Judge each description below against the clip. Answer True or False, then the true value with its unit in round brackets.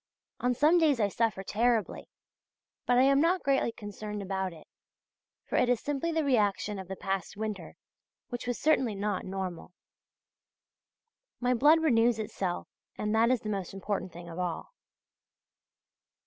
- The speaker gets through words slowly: False (155 wpm)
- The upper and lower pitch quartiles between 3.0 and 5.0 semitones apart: True (4.6 semitones)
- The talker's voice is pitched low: False (220 Hz)